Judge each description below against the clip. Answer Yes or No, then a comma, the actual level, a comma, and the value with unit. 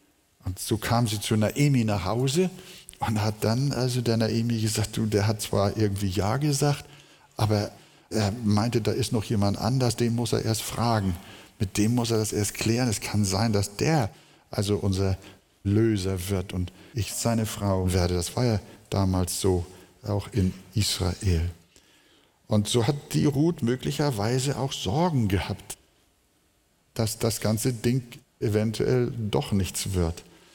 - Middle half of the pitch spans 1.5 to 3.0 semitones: No, average, 3.4 semitones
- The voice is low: Yes, low, 110 Hz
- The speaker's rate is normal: Yes, average, 160 wpm